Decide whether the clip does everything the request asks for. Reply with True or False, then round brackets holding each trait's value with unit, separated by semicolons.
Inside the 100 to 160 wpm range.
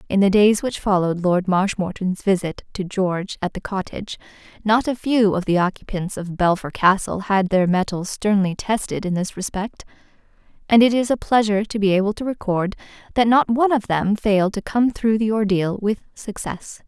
False (190 wpm)